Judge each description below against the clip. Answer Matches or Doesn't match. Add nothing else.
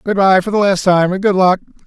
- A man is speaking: Matches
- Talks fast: Matches